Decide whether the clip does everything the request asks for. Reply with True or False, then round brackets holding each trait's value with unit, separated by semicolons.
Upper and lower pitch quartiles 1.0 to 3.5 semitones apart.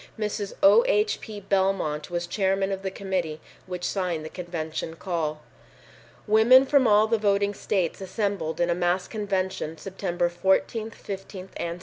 True (3.1 semitones)